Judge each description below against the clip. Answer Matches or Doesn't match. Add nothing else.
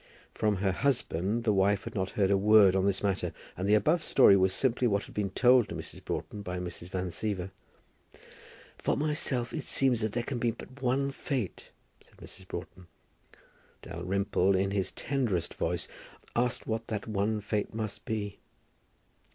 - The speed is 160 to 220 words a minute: Matches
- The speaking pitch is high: Doesn't match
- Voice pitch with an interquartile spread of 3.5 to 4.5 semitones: Matches